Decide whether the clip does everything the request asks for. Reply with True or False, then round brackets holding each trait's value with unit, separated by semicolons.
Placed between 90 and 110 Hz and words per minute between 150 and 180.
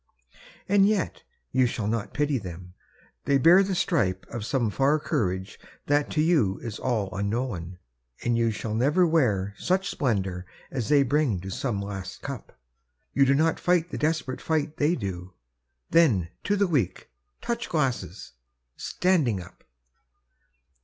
False (130 Hz; 155 wpm)